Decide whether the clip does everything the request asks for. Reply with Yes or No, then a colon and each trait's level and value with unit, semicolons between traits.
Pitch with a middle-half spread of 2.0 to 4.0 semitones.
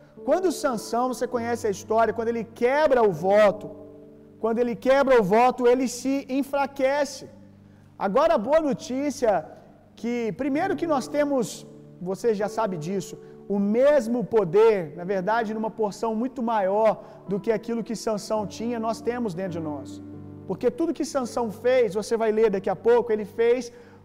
Yes: average, 3.2 semitones